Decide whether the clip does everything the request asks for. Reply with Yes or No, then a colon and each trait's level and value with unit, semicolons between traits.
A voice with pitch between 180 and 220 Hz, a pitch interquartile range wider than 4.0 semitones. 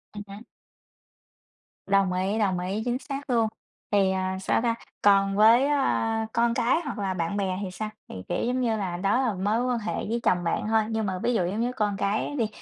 No: high, 210 Hz; average, 3.5 semitones